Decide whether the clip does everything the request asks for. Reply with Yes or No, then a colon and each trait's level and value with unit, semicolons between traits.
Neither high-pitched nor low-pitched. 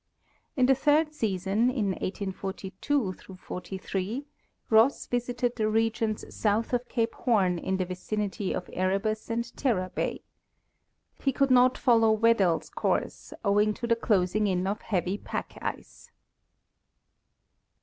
No: high, 215 Hz